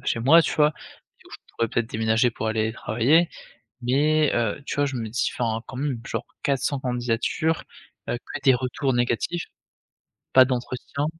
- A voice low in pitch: Yes, low, 125 Hz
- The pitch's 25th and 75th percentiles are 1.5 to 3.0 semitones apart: No, average, 3.7 semitones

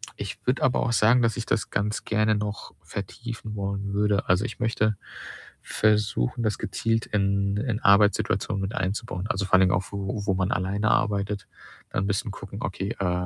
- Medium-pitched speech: No, low, 100 Hz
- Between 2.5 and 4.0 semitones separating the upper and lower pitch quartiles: No, narrow, 1.8 semitones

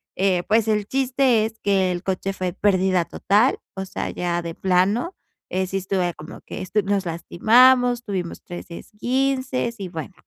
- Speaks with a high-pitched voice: Yes, high, 195 Hz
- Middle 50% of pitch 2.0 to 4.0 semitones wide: No, average, 4.5 semitones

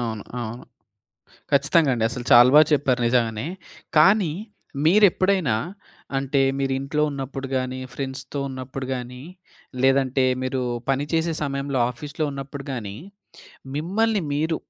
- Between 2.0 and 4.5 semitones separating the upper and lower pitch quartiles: Yes, average, 2.9 semitones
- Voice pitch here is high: No, low, 135 Hz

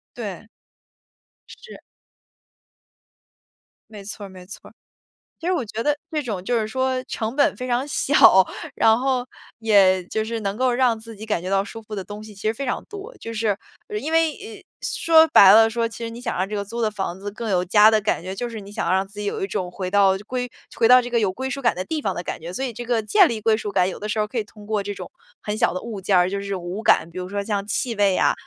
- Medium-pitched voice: No, high, 215 Hz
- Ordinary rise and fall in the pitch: Yes, average, 3.5 semitones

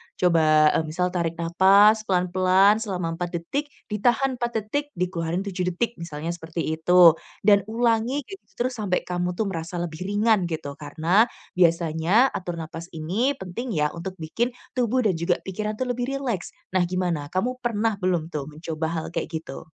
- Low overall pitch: No, medium, 180 Hz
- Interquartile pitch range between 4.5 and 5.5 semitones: Yes, average, 4.8 semitones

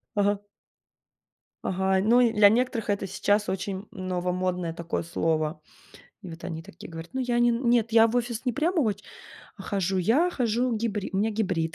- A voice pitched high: Yes, high, 205 Hz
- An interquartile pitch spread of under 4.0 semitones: No, average, 4.4 semitones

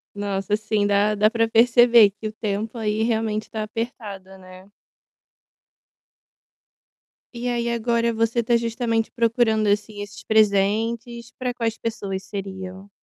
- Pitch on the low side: No, high, 220 Hz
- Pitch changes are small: Yes, narrow, 2.3 semitones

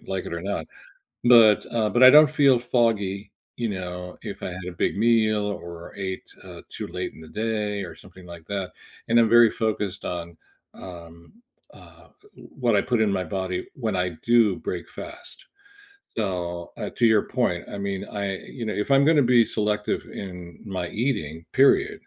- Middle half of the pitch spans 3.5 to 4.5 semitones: Yes, average, 4.1 semitones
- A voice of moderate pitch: No, low, 100 Hz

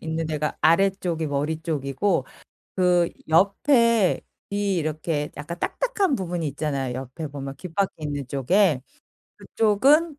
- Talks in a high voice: No, medium, 165 Hz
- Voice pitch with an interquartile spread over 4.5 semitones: Yes, average, 5.2 semitones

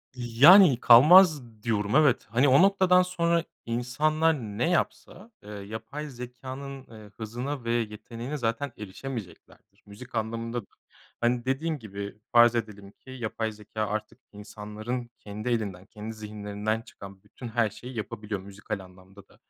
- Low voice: Yes, low, 115 Hz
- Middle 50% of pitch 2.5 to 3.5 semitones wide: No, average, 3.9 semitones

